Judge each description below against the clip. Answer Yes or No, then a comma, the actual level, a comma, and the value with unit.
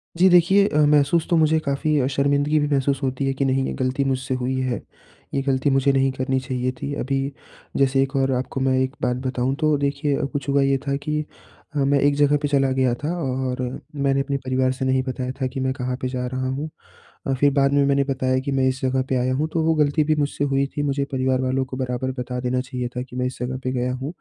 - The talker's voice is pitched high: No, low, 135 Hz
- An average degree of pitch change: No, narrow, 1.7 semitones